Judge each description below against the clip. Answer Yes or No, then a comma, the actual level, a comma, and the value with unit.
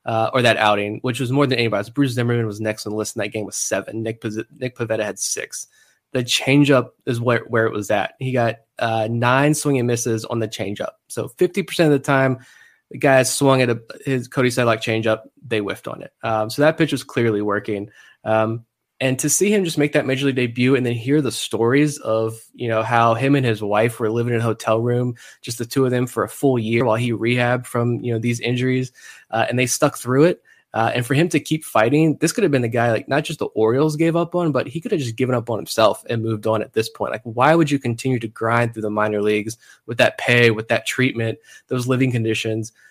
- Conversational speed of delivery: No, fast, 250 wpm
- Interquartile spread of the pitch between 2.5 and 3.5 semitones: Yes, average, 3.1 semitones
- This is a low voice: Yes, low, 120 Hz